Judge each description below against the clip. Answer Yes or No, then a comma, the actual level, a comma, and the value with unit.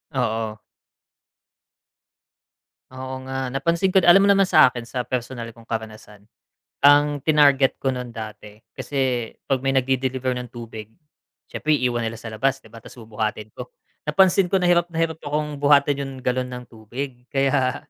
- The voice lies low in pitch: Yes, low, 130 Hz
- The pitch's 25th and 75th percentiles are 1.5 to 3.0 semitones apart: No, average, 3.7 semitones